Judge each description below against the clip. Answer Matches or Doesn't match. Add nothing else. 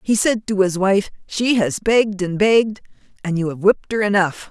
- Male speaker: Doesn't match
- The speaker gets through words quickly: Matches